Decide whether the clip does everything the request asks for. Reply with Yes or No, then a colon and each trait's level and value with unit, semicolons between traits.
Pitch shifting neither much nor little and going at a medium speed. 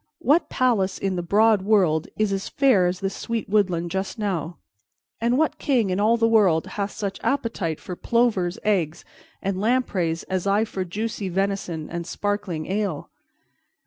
Yes: average, 3.7 semitones; average, 165 wpm